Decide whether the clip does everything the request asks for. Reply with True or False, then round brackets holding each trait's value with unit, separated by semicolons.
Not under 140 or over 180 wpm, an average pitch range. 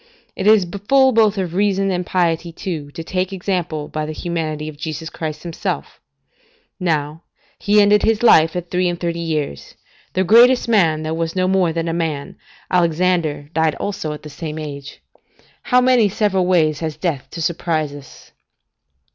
True (170 wpm; 3.5 semitones)